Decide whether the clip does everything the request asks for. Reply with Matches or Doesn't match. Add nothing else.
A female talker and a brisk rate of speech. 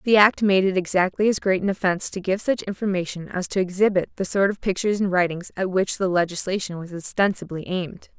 Matches